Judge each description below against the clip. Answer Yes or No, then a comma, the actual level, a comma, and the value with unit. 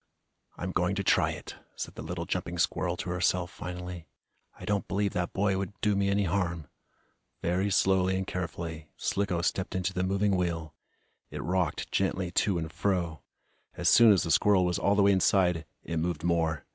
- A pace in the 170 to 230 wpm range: Yes, average, 185 wpm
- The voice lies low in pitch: Yes, very low, 90 Hz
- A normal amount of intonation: No, narrow, 2.3 semitones